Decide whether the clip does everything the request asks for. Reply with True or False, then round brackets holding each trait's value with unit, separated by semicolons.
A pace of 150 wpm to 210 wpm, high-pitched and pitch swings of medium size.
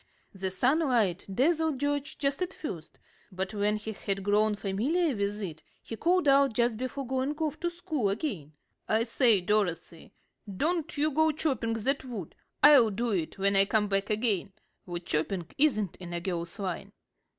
False (170 wpm; 220 Hz; 6.4 semitones)